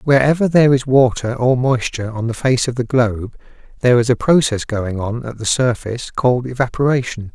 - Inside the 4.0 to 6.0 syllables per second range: Yes, 5.7 syllables/s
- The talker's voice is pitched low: Yes, low, 125 Hz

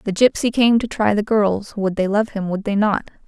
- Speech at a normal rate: No, fast, 255 wpm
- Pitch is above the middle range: Yes, high, 210 Hz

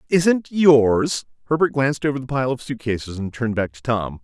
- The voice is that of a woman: No, male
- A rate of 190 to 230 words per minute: Yes, average, 200 wpm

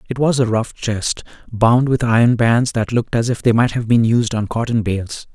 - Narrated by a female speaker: No, male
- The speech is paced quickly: Yes, fast, 235 wpm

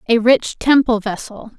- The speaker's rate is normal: Yes, average, 150 wpm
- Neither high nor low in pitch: No, high, 230 Hz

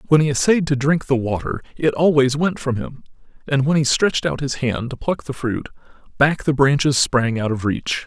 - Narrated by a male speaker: Yes, male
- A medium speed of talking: No, fast, 225 wpm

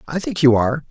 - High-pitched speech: No, medium, 145 Hz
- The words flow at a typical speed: No, fast, 265 wpm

